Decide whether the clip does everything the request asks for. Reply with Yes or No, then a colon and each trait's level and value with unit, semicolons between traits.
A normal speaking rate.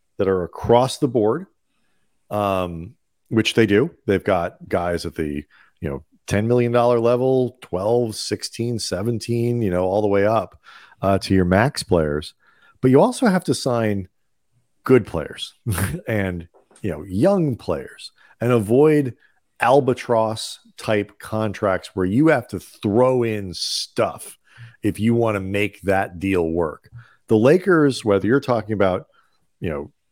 Yes: average, 145 wpm